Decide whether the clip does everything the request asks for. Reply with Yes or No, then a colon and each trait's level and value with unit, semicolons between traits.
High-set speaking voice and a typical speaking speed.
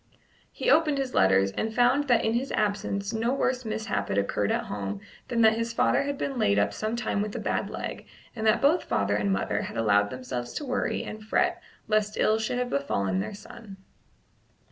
No: high, 215 Hz; fast, 210 wpm